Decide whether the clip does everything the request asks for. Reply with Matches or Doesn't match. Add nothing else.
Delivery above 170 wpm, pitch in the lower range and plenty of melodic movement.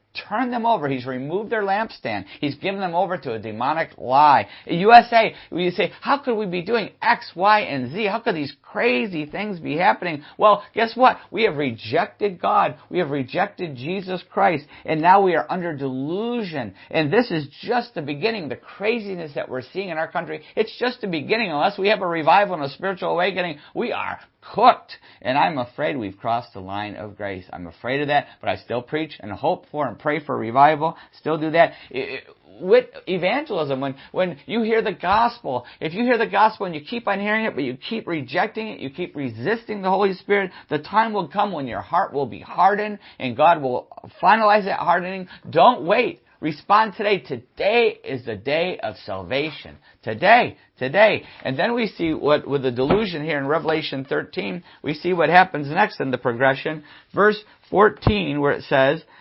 Doesn't match